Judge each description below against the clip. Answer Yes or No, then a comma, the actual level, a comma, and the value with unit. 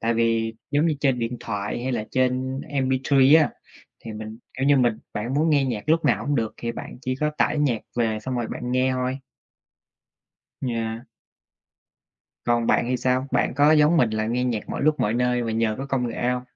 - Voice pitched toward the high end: No, low, 125 Hz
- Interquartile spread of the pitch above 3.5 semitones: No, average, 2.9 semitones